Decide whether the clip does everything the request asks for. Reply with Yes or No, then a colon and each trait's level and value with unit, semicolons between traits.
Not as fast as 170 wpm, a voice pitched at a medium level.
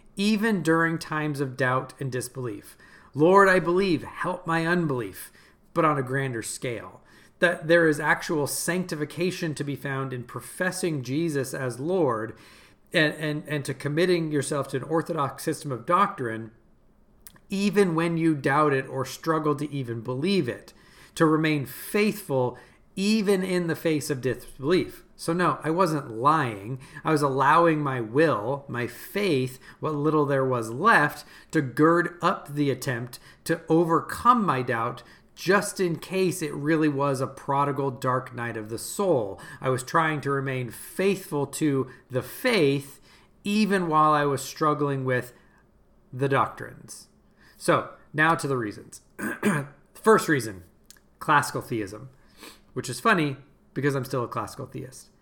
Yes: average, 150 wpm; medium, 150 Hz